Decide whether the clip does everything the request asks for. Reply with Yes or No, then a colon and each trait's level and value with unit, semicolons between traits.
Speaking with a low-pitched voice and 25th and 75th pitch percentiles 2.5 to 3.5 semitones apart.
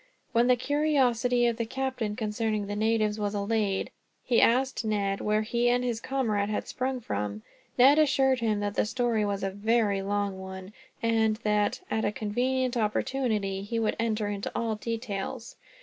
No: high, 220 Hz; average, 3.0 semitones